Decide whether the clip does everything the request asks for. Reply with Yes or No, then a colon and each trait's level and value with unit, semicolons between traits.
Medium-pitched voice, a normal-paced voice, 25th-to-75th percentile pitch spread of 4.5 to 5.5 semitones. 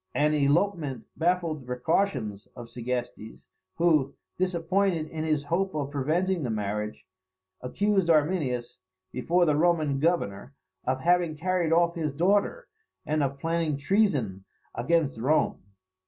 No: medium, 155 Hz; slow, 125 wpm; average, 4.8 semitones